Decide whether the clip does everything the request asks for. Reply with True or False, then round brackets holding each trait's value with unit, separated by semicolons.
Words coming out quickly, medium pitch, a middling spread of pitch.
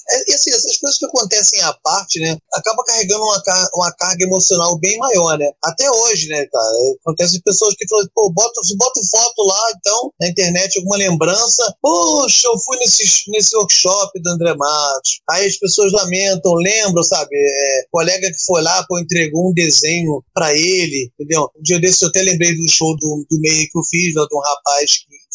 True (195 wpm; 180 Hz; 4.3 semitones)